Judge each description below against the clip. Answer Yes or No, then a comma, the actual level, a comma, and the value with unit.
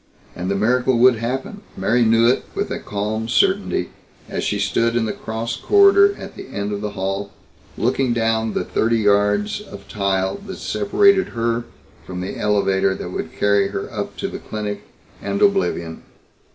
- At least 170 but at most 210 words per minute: Yes, average, 175 wpm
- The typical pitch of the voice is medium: No, low, 110 Hz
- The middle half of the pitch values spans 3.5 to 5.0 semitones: No, average, 3.0 semitones